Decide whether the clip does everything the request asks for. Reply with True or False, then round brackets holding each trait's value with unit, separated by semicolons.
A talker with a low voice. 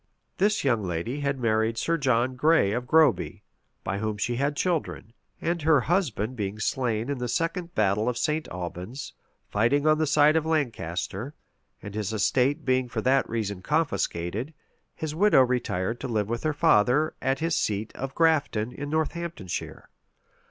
True (130 Hz)